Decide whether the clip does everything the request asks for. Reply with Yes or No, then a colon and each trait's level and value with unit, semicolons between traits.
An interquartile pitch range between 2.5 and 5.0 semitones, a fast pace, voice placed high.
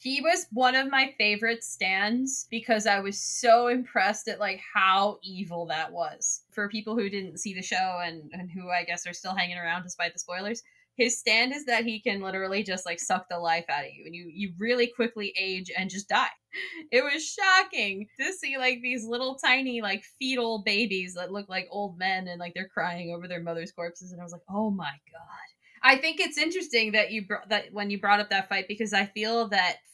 Yes: average, 4.4 semitones; fast, 225 wpm; high, 205 Hz